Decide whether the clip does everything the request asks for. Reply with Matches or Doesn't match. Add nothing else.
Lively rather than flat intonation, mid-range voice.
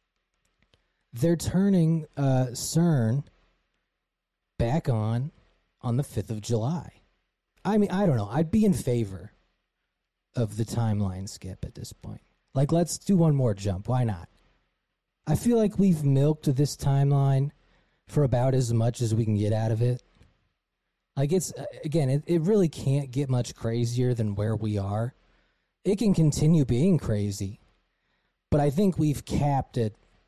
Doesn't match